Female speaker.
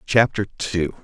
No: male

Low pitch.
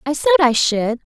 No: high, 235 Hz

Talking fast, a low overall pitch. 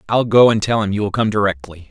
Yes: fast, 285 wpm; low, 105 Hz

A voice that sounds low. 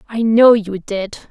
No: high, 215 Hz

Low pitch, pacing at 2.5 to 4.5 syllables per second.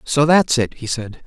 Yes: low, 130 Hz; 4.3 syllables/s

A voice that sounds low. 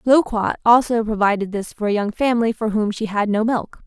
No: high, 220 Hz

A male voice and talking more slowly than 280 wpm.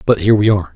No: male; fast, 320 wpm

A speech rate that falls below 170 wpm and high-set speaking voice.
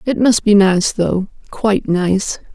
Yes: average, 140 wpm; high, 200 Hz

